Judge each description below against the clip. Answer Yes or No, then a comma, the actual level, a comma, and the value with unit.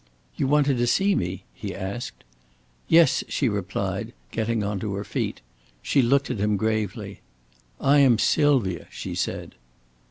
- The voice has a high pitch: No, low, 110 Hz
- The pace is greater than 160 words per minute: No, average, 150 wpm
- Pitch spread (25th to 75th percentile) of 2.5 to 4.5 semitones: No, wide, 5.4 semitones